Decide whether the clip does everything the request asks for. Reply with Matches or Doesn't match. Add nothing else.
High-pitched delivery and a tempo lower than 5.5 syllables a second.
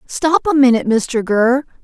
Matches